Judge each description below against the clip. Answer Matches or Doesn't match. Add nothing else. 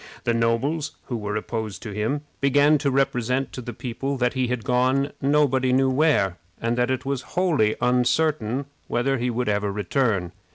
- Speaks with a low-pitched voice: Matches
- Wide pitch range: Doesn't match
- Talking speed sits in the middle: Matches